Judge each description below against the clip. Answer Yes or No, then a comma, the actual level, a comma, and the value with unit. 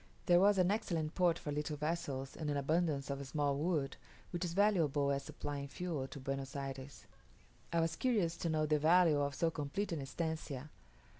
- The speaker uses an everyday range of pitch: Yes, average, 3.4 semitones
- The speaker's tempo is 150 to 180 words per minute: No, average, 190 wpm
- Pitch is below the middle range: No, medium, 155 Hz